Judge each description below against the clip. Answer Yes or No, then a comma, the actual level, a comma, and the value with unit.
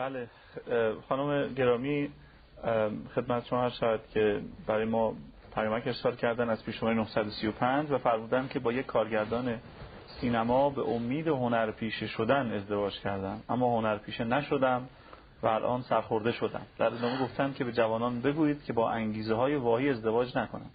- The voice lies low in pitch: Yes, low, 120 Hz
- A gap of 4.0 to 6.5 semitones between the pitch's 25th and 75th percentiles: No, average, 2.7 semitones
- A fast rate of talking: No, average, 145 wpm